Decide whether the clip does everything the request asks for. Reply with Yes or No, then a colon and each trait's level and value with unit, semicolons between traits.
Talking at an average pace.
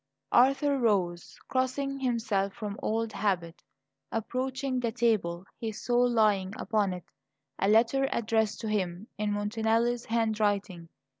No: slow, 125 wpm